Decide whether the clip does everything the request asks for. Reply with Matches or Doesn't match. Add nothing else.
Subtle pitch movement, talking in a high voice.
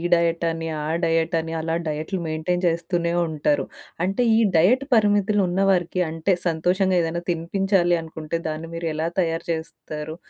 Doesn't match